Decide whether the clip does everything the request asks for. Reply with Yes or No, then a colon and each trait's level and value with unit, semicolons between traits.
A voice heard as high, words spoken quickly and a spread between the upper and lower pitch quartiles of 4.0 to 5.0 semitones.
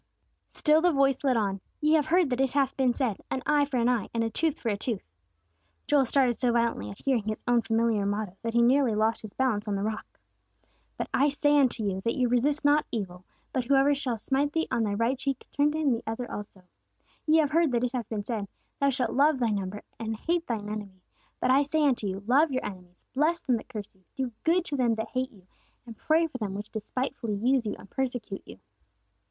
Yes: high, 245 Hz; fast, 240 wpm; average, 4.5 semitones